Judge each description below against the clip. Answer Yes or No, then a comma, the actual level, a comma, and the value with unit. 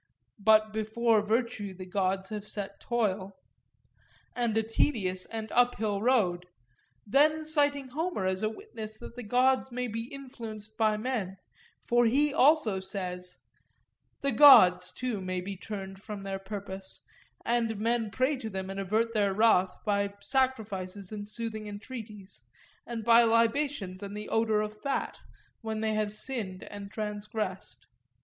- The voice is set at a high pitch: Yes, high, 215 Hz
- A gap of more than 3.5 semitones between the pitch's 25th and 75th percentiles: No, average, 3.2 semitones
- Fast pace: No, average, 145 wpm